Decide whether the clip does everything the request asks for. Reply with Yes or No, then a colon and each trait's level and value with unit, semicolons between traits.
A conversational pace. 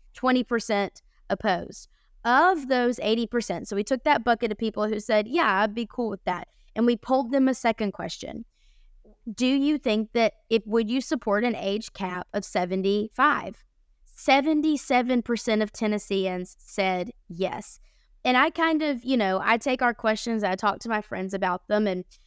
Yes: average, 170 wpm